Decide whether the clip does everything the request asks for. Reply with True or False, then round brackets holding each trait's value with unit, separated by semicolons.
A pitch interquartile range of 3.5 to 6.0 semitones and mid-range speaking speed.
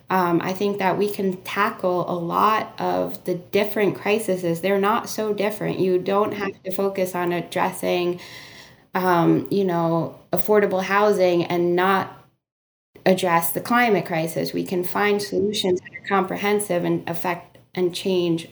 False (2.6 semitones; 150 wpm)